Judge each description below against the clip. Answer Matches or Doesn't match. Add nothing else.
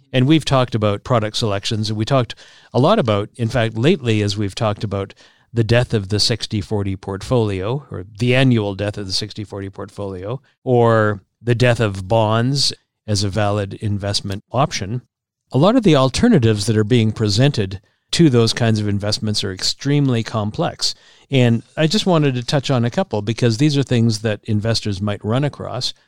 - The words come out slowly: Doesn't match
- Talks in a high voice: Doesn't match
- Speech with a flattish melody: Doesn't match